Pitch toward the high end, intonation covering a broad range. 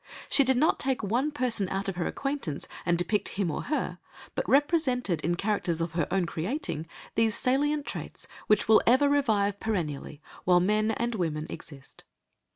Yes: high, 210 Hz; wide, 7.2 semitones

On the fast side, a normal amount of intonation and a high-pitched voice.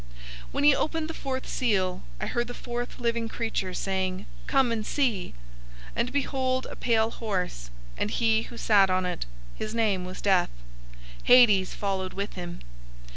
No: average, 175 wpm; average, 4.5 semitones; high, 215 Hz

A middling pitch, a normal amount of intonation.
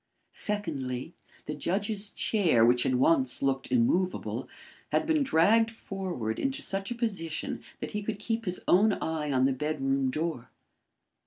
No: medium, 165 Hz; wide, 7.6 semitones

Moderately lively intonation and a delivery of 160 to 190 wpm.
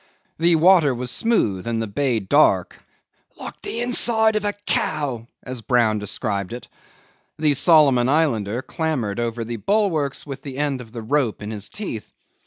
No: wide, 6.0 semitones; average, 165 wpm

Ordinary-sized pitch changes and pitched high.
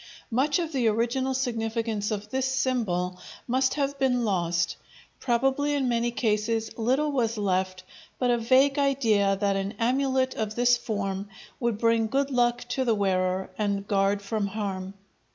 Yes: average, 4.4 semitones; high, 230 Hz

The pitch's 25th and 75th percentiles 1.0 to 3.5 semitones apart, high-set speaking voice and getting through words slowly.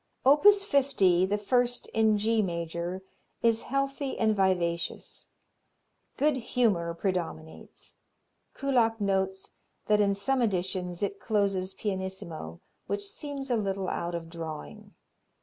No: average, 4.4 semitones; high, 200 Hz; slow, 115 wpm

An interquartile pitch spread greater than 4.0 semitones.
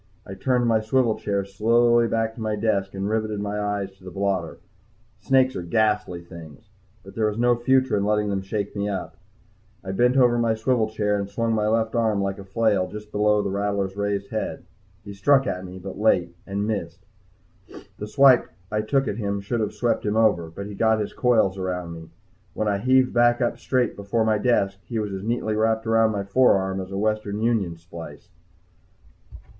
No: narrow, 2.5 semitones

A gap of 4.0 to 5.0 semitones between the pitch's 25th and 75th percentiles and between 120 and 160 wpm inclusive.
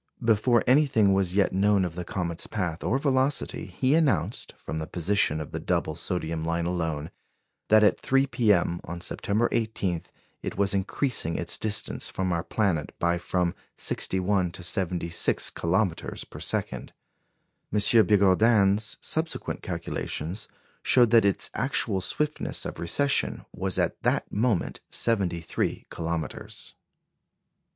Yes: average, 4.5 semitones; slow, 135 wpm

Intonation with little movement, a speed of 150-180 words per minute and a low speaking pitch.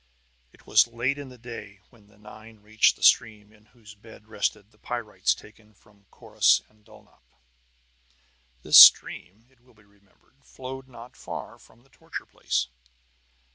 Yes: narrow, 2.3 semitones; average, 160 wpm; low, 110 Hz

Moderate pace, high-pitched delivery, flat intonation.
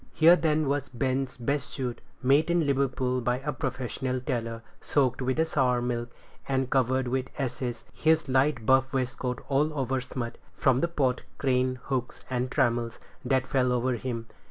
No: average, 160 wpm; low, 130 Hz; narrow, 1.7 semitones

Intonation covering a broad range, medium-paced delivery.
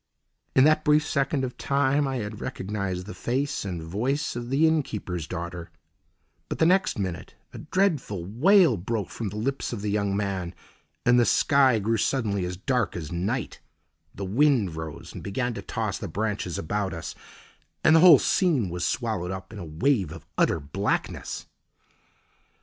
Yes: wide, 6.7 semitones; average, 175 wpm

